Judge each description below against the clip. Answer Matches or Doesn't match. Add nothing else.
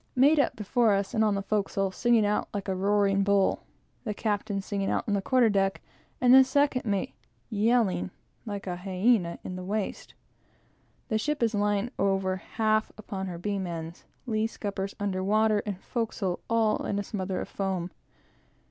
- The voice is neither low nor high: Doesn't match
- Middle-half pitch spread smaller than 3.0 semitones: Matches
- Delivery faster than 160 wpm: Matches